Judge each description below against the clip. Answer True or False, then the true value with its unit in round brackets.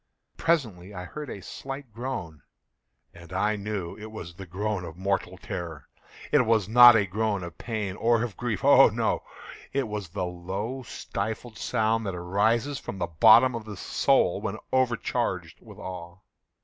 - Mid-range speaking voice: False (105 Hz)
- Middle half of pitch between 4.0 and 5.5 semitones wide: True (4.3 semitones)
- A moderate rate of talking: True (160 wpm)